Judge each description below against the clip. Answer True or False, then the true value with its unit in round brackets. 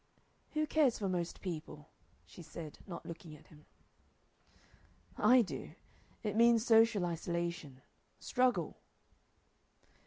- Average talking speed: False (105 wpm)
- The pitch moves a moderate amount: False (5.8 semitones)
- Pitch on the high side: False (180 Hz)